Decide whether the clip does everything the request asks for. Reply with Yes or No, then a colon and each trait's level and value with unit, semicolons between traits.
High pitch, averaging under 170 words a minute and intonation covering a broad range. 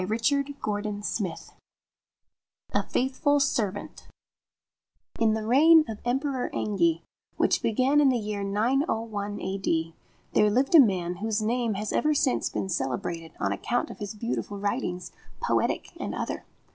No: high, 215 Hz; average, 140 wpm; average, 4.7 semitones